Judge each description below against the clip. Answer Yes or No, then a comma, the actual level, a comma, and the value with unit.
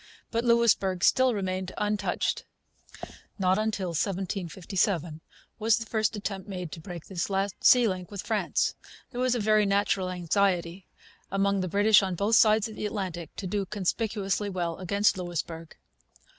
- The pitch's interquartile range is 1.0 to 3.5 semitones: Yes, narrow, 2.6 semitones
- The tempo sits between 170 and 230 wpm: No, average, 155 wpm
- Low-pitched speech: No, high, 195 Hz